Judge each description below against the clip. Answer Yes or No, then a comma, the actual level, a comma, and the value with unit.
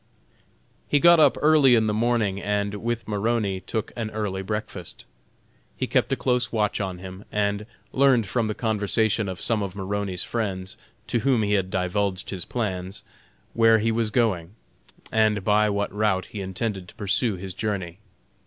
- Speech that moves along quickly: No, average, 170 wpm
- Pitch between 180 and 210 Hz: No, low, 105 Hz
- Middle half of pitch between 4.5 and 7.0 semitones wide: No, average, 2.9 semitones